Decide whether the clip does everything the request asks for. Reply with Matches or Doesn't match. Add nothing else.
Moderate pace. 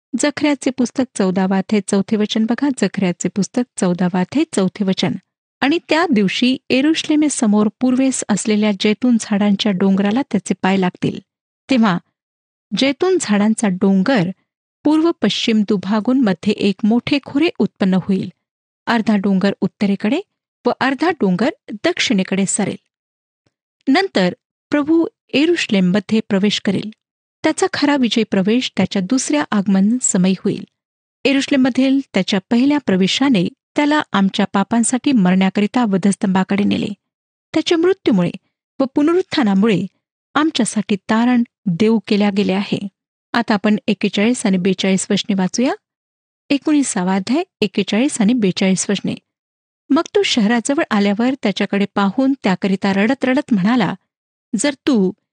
Matches